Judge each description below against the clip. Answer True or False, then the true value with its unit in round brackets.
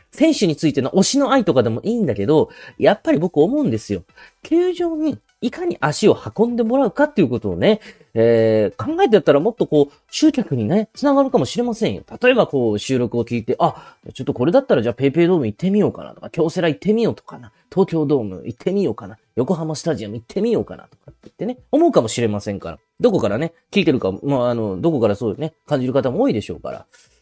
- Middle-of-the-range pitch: True (160 Hz)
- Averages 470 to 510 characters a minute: True (485 characters per minute)